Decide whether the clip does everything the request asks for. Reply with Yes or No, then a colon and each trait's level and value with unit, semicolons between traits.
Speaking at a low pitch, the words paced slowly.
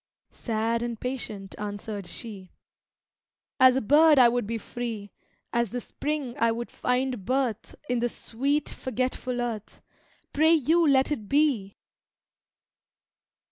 No: high, 240 Hz; slow, 130 wpm